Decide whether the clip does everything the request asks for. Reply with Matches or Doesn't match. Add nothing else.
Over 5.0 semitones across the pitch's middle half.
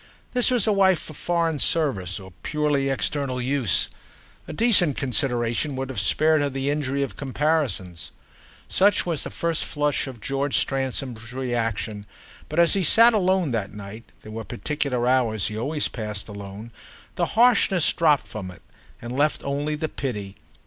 Matches